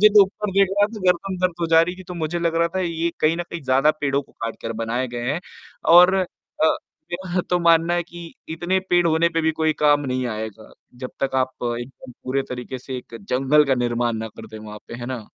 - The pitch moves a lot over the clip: Yes, wide, 5.8 semitones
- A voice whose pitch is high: No, medium, 155 Hz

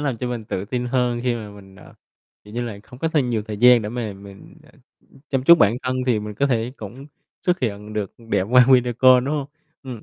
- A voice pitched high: No, low, 120 Hz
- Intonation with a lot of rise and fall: No, average, 3.2 semitones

